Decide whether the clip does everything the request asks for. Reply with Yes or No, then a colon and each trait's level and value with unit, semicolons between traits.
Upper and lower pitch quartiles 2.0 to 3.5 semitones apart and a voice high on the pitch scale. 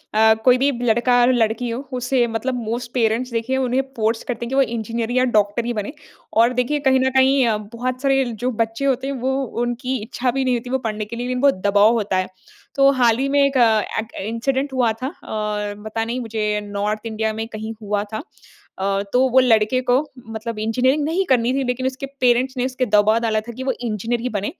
Yes: average, 2.8 semitones; high, 240 Hz